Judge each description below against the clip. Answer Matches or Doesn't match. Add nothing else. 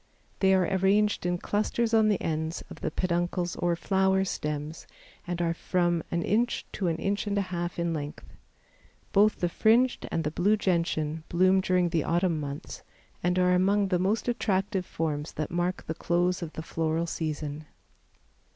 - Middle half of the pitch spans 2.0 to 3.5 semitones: Matches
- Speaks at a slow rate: Doesn't match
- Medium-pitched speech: Matches